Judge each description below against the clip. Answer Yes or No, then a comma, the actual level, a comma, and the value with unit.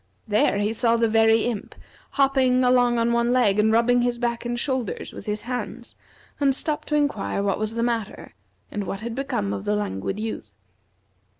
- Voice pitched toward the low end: No, high, 235 Hz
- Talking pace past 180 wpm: Yes, average, 190 wpm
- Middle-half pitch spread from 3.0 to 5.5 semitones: No, narrow, 2.6 semitones